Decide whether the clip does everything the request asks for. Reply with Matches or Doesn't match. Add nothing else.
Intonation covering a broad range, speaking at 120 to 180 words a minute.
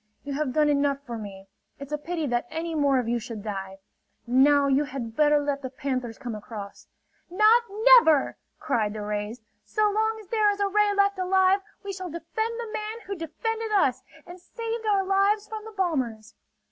Doesn't match